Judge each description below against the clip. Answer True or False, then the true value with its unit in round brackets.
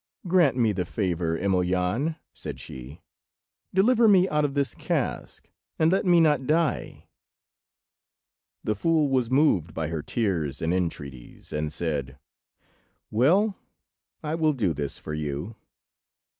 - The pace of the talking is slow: True (130 wpm)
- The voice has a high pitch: False (105 Hz)